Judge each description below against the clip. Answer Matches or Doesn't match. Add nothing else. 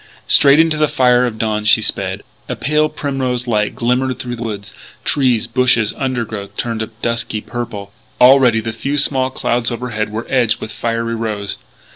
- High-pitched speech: Doesn't match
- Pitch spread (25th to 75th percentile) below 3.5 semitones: Matches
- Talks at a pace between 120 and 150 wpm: Doesn't match